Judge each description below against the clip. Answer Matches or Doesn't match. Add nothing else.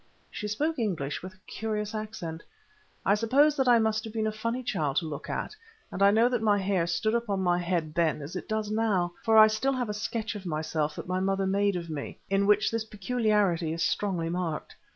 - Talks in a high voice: Matches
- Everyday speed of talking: Doesn't match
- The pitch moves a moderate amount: Matches